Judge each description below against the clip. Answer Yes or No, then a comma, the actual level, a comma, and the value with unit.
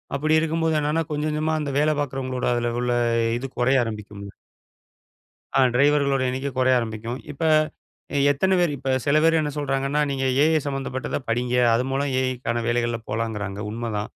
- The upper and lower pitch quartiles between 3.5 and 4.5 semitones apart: Yes, average, 3.8 semitones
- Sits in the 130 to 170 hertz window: Yes, low, 135 Hz